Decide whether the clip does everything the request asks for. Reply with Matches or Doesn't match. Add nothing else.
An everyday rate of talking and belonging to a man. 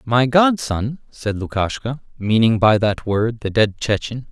Matches